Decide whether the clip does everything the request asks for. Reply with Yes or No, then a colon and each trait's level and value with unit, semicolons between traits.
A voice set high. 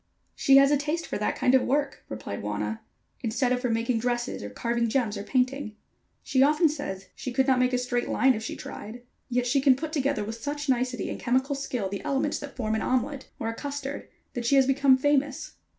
Yes: very high, 255 Hz